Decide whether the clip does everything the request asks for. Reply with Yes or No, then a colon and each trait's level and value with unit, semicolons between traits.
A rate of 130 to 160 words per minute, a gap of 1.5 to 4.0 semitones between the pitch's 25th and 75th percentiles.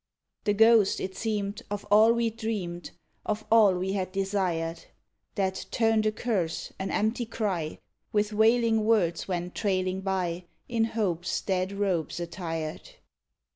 Yes: slow, 135 wpm; average, 3.2 semitones